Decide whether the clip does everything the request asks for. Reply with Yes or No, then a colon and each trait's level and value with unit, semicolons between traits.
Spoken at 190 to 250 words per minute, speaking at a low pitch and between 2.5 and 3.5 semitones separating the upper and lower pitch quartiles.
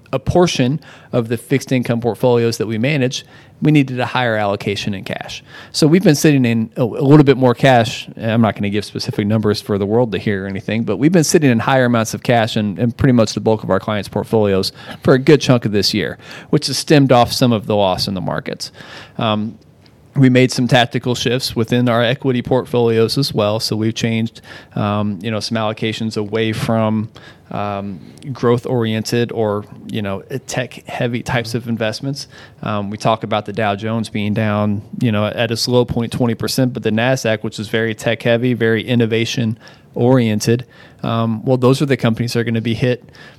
Yes: fast, 205 wpm; low, 115 Hz; average, 2.9 semitones